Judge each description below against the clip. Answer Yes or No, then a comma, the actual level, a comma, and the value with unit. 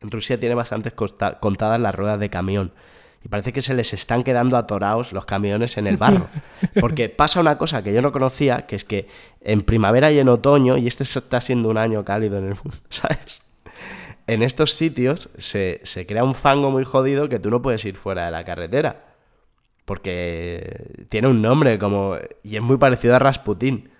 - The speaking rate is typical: No, fast, 200 wpm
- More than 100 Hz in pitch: Yes, low, 120 Hz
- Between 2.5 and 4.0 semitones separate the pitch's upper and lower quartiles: No, average, 4.4 semitones